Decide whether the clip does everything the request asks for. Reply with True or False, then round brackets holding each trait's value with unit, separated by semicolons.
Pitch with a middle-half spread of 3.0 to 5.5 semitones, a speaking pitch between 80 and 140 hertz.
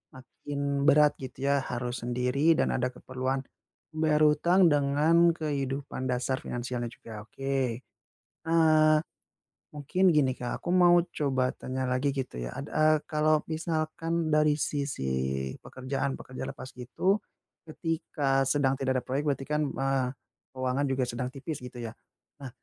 True (3.3 semitones; 135 Hz)